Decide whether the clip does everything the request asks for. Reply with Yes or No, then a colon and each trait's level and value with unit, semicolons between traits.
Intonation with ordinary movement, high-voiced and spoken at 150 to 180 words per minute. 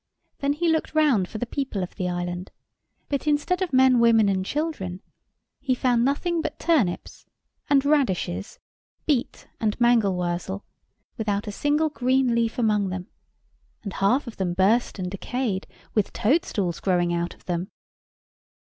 No: wide, 6.7 semitones; high, 225 Hz; average, 160 wpm